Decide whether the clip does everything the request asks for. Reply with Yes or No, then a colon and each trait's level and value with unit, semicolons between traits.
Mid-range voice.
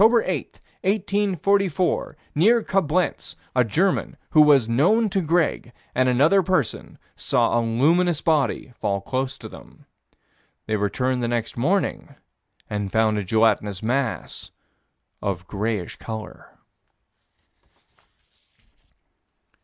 No: low, 130 Hz